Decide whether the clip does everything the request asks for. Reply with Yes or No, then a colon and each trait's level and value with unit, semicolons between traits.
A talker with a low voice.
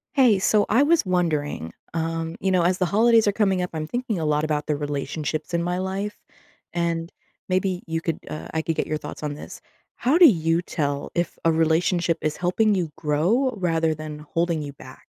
No: medium, 170 Hz